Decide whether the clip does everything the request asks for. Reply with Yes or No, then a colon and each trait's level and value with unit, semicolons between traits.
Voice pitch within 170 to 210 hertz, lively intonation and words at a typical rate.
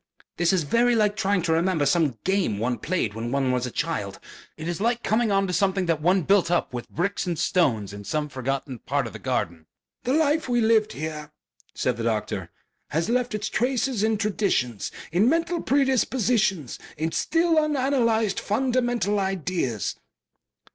Yes: high, 190 Hz; wide, 8.4 semitones; average, 170 wpm